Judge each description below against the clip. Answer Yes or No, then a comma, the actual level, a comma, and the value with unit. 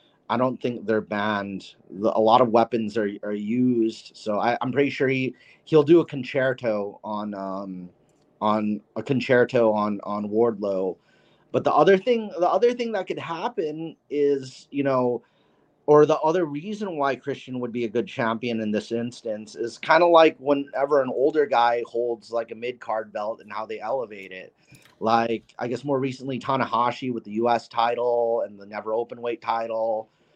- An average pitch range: Yes, average, 4.1 semitones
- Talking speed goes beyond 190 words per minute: No, average, 180 wpm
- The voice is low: Yes, low, 120 Hz